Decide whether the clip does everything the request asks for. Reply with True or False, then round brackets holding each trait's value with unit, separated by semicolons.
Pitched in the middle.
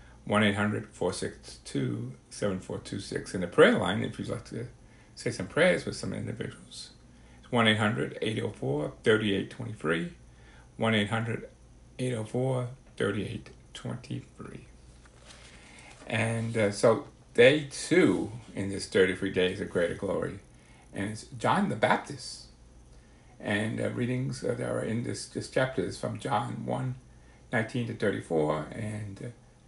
False (100 Hz)